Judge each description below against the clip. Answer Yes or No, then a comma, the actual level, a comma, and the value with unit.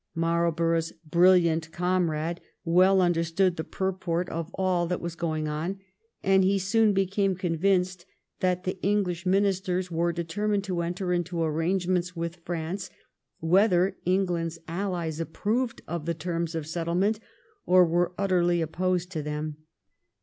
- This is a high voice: No, medium, 175 Hz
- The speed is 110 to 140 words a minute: Yes, slow, 135 wpm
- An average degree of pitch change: No, narrow, 2.0 semitones